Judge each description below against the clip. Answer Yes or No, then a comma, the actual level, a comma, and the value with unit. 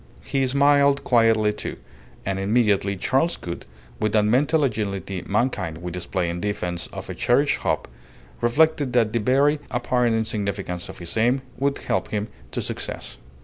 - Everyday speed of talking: Yes, average, 155 wpm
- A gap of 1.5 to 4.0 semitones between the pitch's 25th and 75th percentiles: No, average, 5.1 semitones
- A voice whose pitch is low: Yes, low, 110 Hz